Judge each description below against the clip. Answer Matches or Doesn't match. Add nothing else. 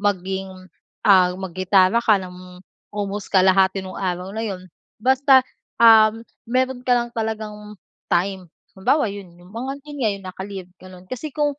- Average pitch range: Matches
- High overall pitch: Matches